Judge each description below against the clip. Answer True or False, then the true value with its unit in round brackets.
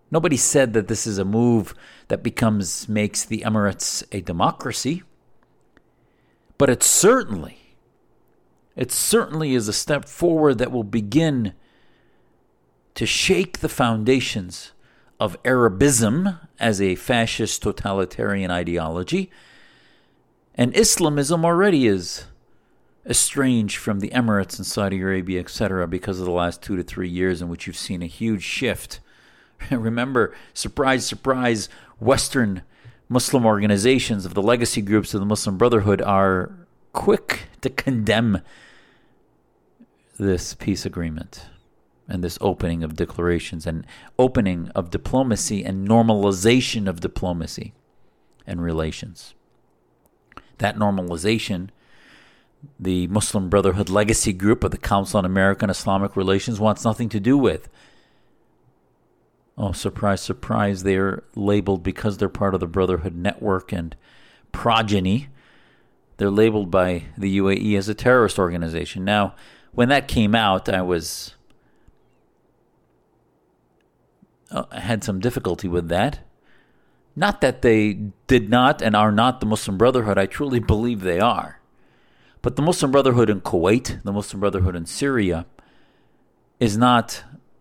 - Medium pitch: False (105 Hz)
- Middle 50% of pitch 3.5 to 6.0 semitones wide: True (4.1 semitones)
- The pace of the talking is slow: True (125 wpm)